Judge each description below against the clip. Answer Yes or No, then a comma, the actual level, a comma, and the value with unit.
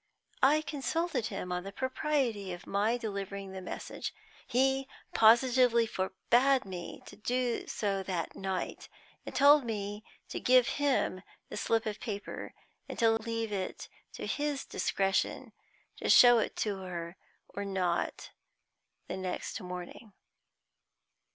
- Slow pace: Yes, slow, 130 wpm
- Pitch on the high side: Yes, high, 220 Hz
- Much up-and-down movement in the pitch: No, average, 4.8 semitones